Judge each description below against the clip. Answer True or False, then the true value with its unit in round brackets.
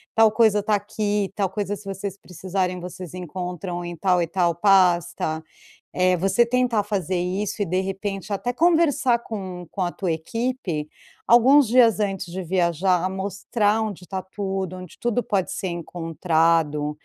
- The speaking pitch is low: False (190 Hz)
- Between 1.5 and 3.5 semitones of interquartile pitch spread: True (2.9 semitones)